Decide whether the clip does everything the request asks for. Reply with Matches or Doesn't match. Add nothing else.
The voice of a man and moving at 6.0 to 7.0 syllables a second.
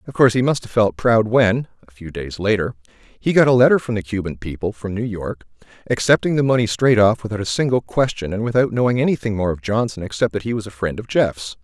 Matches